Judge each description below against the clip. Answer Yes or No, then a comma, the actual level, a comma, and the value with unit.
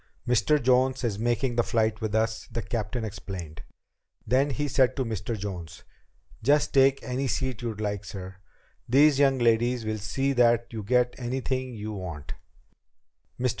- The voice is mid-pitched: No, low, 120 Hz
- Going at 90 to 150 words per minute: No, average, 160 wpm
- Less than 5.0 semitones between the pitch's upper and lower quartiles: Yes, average, 3.4 semitones